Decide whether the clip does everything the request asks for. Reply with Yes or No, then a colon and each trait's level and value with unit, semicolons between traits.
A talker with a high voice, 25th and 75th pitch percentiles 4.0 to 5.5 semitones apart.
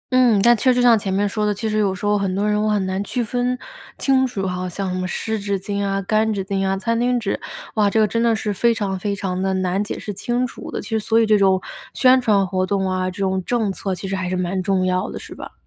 No: high, 200 Hz; average, 2.7 semitones